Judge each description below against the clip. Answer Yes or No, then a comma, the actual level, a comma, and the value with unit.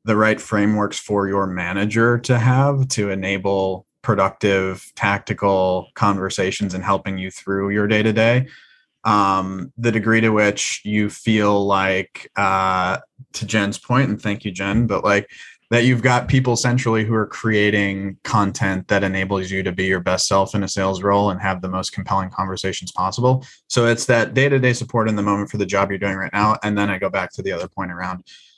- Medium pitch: No, low, 100 Hz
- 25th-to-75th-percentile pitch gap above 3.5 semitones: No, average, 2.7 semitones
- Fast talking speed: No, average, 195 wpm